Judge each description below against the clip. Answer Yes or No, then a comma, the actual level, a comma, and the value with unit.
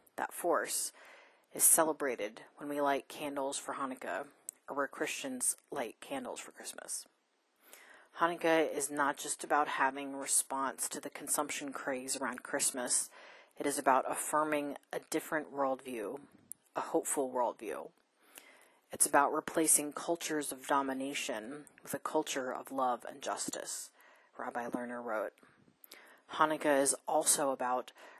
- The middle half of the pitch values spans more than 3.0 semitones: No, average, 2.7 semitones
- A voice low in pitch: No, medium, 145 Hz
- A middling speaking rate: No, slow, 130 wpm